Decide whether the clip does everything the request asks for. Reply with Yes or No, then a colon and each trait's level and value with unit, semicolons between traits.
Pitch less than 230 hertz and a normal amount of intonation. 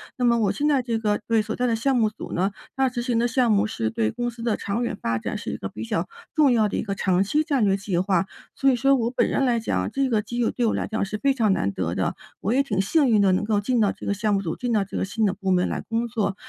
Yes: high, 220 Hz; average, 3.5 semitones